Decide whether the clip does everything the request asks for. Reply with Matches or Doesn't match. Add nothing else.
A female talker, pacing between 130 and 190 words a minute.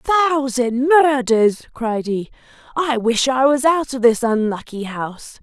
Matches